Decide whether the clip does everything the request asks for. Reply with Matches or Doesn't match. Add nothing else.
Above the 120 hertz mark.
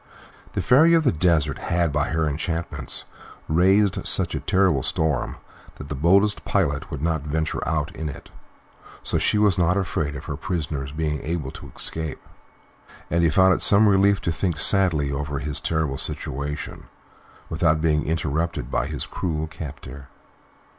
Doesn't match